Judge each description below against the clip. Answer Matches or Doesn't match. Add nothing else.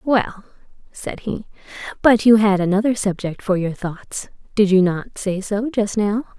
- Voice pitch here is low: Doesn't match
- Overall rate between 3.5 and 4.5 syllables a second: Matches